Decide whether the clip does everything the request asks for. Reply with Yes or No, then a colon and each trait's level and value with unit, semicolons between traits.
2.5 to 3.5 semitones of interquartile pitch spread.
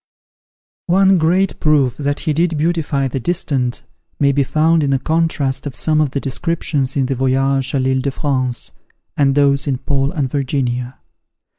Yes: average, 2.8 semitones